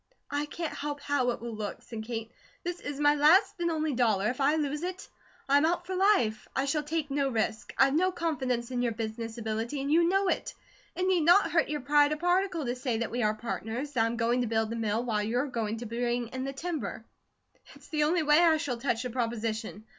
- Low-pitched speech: No, very high, 270 Hz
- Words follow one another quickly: Yes, fast, 235 wpm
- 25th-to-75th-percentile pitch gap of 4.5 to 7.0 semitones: Yes, average, 5.1 semitones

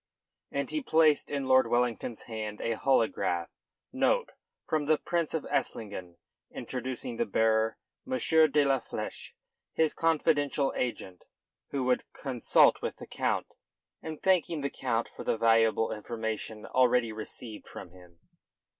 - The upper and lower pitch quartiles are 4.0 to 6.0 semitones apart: Yes, average, 4.8 semitones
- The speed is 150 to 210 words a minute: No, slow, 135 wpm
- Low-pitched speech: Yes, low, 125 Hz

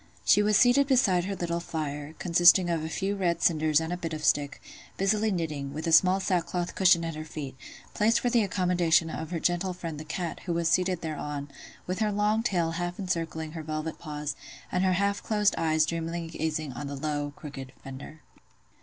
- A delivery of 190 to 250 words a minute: Yes, average, 200 wpm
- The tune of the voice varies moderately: Yes, average, 3.1 semitones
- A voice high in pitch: No, medium, 170 Hz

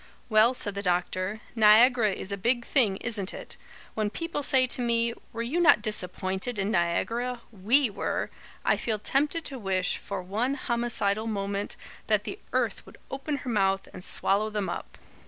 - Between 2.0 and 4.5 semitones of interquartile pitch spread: Yes, average, 3.7 semitones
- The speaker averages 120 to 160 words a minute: No, average, 175 wpm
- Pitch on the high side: Yes, high, 215 Hz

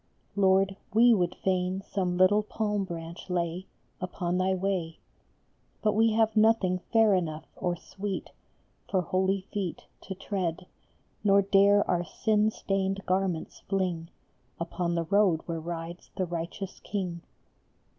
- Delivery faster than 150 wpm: No, slow, 135 wpm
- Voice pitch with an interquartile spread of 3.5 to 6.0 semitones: No, narrow, 2.4 semitones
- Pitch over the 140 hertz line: Yes, high, 190 Hz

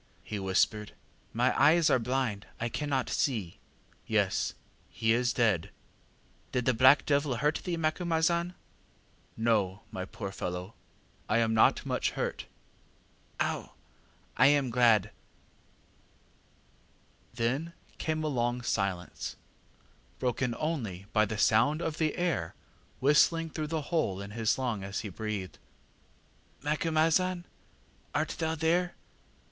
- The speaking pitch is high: No, low, 125 Hz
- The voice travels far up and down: Yes, wide, 6.4 semitones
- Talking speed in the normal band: No, slow, 125 wpm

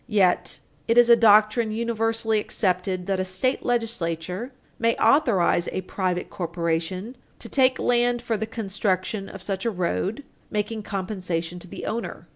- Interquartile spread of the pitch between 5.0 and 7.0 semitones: No, average, 4.0 semitones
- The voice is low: No, high, 210 Hz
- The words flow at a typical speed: Yes, average, 150 wpm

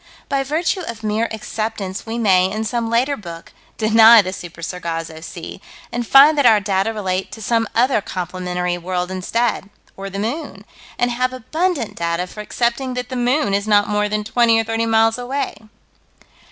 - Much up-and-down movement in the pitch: No, average, 4.2 semitones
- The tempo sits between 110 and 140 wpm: No, average, 180 wpm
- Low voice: No, high, 220 Hz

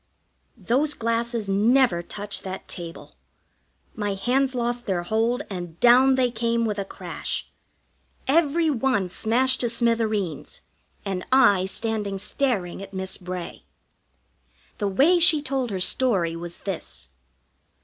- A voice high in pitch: Yes, high, 225 Hz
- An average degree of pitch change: Yes, average, 5.0 semitones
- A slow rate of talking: Yes, slow, 130 wpm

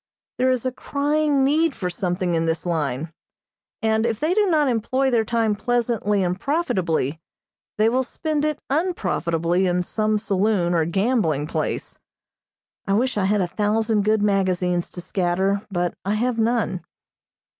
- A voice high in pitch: Yes, high, 210 Hz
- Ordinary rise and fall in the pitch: No, wide, 5.9 semitones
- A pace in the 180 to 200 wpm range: No, average, 155 wpm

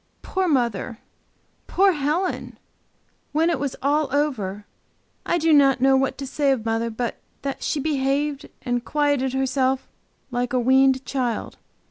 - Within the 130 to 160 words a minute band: Yes, average, 145 wpm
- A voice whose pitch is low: No, very high, 270 Hz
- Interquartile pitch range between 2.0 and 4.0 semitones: Yes, average, 2.8 semitones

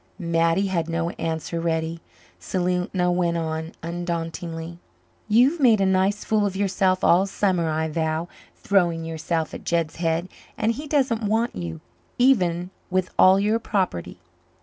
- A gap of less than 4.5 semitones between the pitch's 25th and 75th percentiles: Yes, average, 3.2 semitones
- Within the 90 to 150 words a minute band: Yes, average, 145 wpm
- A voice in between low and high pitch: Yes, medium, 175 Hz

